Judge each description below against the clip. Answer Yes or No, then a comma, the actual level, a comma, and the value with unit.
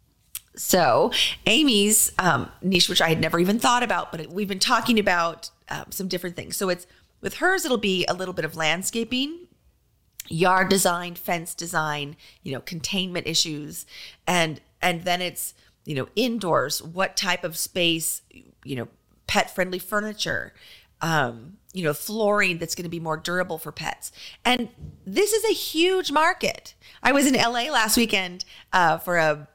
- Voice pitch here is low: No, medium, 180 Hz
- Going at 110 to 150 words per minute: No, average, 170 wpm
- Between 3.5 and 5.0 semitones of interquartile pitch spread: Yes, average, 4.7 semitones